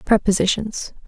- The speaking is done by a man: No, female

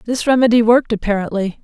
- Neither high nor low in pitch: No, high, 225 Hz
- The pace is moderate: Yes, average, 145 wpm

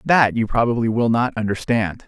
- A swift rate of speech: No, average, 175 wpm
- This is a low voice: Yes, low, 115 Hz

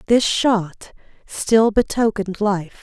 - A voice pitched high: Yes, high, 210 Hz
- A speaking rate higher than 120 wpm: No, slow, 105 wpm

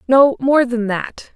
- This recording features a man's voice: No, female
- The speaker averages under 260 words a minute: Yes, slow, 135 wpm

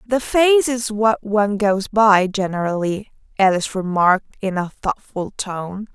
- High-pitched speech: Yes, high, 205 Hz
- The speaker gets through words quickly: No, average, 140 wpm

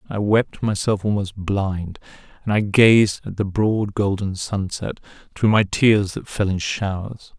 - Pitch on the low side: Yes, low, 100 Hz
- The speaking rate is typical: Yes, average, 165 wpm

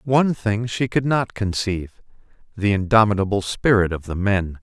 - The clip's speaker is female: No, male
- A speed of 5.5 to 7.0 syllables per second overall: No, 5.0 syllables/s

